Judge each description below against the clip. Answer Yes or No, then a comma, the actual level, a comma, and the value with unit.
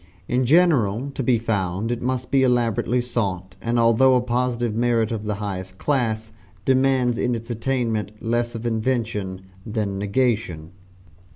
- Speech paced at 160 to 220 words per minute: No, average, 150 wpm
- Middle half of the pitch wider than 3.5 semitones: No, average, 2.9 semitones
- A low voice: Yes, low, 115 Hz